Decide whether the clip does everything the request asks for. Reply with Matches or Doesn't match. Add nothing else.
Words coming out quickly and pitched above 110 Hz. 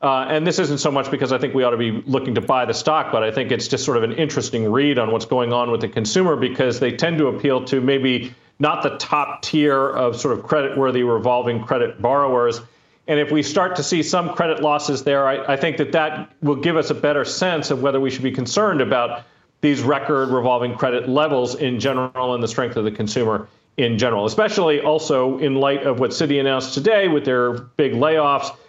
Matches